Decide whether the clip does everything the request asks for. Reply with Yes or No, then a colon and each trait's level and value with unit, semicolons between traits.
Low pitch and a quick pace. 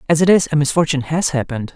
No: medium, 150 Hz; fast, 240 wpm